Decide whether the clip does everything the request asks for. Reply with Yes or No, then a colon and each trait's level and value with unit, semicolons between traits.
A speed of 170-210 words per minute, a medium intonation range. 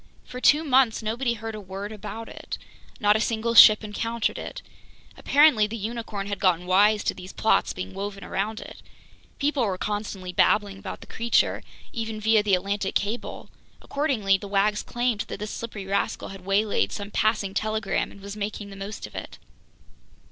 No: average, 175 wpm; narrow, 2.3 semitones